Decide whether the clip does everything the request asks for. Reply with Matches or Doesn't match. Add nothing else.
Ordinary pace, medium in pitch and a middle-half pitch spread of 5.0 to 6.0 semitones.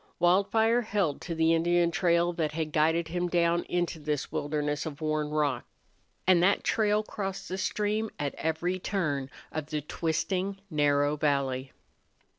Doesn't match